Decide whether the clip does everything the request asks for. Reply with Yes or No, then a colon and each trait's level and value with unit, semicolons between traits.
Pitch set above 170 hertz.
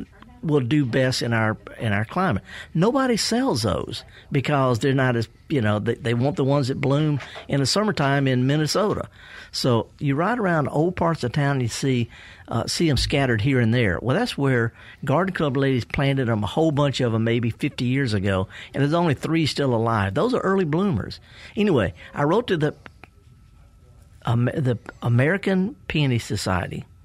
No: low, 135 Hz